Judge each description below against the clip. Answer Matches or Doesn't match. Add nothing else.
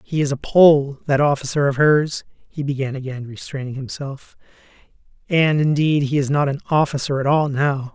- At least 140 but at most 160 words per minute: Doesn't match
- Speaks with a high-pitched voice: Doesn't match